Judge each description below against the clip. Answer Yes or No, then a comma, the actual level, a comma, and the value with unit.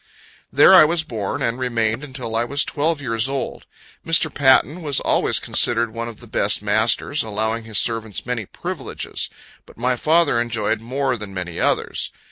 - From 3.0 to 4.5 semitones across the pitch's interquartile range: Yes, average, 3.8 semitones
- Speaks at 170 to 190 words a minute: Yes, average, 175 wpm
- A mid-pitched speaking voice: No, low, 120 Hz